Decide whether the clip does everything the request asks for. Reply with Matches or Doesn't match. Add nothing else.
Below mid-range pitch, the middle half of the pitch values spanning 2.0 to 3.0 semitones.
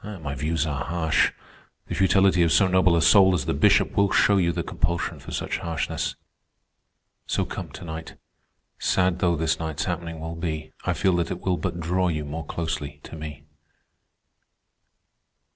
Matches